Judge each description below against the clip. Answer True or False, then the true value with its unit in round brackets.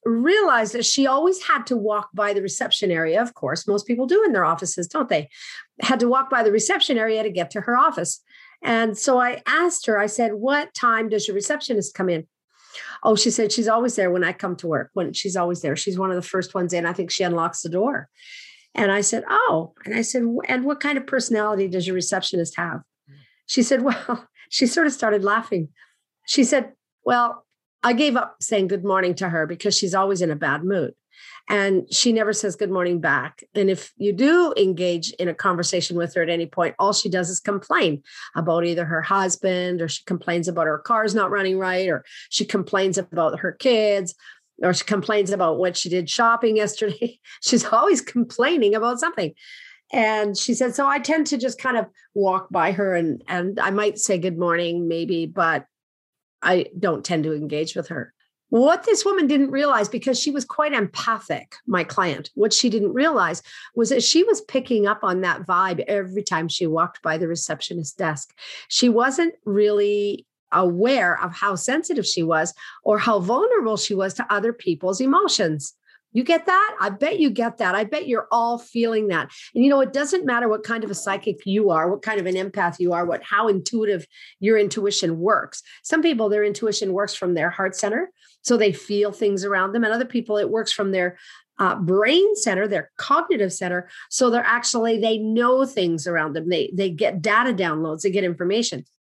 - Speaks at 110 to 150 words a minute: False (205 wpm)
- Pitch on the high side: True (205 Hz)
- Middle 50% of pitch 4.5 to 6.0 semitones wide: True (4.9 semitones)